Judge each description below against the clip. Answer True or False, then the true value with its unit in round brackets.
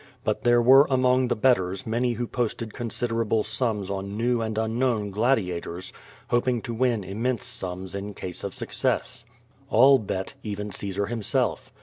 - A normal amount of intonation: True (3.4 semitones)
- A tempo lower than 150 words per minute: False (155 wpm)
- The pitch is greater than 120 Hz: False (115 Hz)